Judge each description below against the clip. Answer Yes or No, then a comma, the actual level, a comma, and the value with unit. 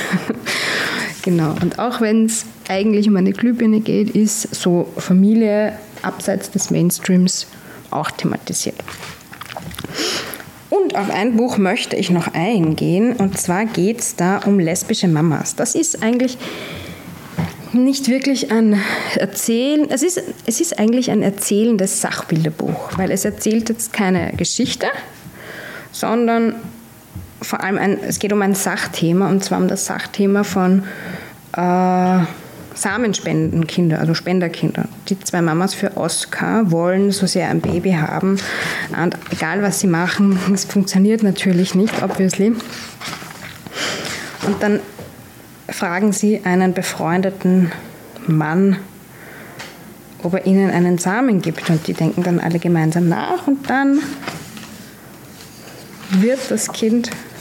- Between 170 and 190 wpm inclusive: No, slow, 125 wpm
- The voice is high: Yes, high, 195 Hz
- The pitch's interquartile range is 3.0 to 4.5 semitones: Yes, average, 3.3 semitones